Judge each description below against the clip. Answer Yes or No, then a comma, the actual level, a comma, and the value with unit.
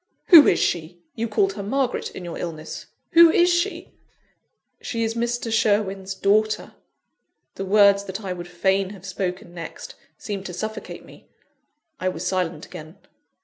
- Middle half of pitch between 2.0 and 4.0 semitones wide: Yes, average, 3.5 semitones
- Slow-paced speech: No, average, 160 wpm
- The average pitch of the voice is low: No, high, 195 Hz